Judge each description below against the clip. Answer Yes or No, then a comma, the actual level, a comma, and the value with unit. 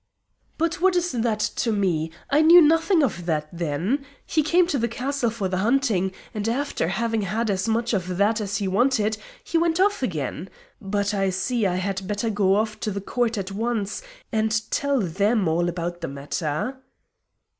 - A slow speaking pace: No, average, 190 wpm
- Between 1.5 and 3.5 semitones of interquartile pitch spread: No, average, 5.0 semitones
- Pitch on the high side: Yes, high, 215 Hz